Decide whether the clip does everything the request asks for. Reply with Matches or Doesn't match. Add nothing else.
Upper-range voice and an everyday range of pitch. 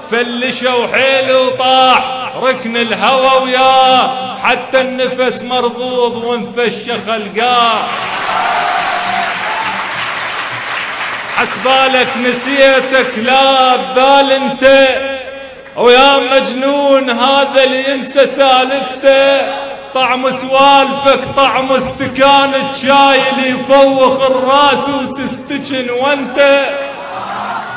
Doesn't match